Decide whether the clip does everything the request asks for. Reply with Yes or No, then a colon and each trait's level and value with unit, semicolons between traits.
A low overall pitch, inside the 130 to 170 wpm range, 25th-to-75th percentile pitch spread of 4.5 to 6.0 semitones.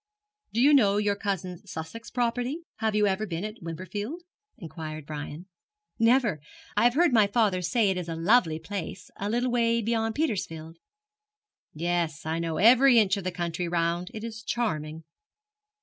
No: high, 200 Hz; average, 165 wpm; wide, 5.6 semitones